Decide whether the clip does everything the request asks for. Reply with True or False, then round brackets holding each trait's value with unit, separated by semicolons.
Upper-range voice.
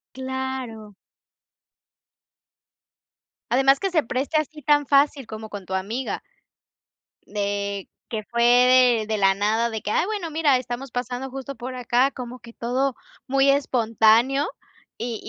True (250 Hz)